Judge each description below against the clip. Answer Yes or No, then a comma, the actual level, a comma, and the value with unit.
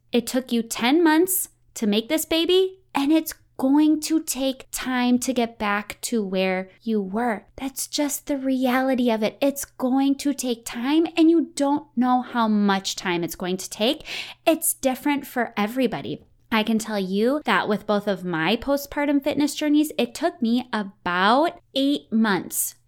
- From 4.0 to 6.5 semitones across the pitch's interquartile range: Yes, average, 5.1 semitones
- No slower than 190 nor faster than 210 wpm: No, average, 175 wpm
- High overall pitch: Yes, very high, 250 Hz